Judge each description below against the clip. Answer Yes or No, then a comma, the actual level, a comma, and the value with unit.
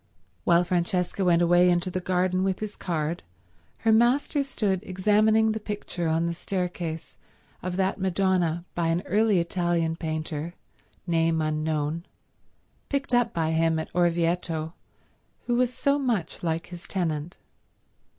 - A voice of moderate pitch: Yes, medium, 175 Hz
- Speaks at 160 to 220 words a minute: No, average, 140 wpm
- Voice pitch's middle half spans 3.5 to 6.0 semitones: No, average, 3.1 semitones